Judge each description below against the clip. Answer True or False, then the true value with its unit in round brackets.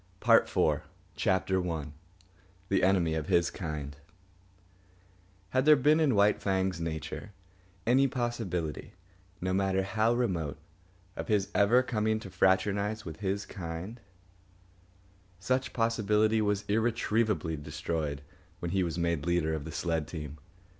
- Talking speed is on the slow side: True (130 wpm)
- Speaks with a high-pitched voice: False (95 Hz)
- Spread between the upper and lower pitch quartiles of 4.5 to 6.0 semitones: True (4.8 semitones)